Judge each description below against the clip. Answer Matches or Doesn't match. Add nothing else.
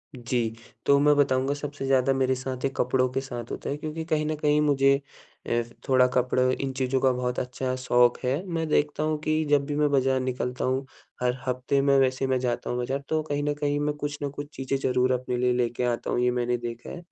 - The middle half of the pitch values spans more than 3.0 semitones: Doesn't match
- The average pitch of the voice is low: Matches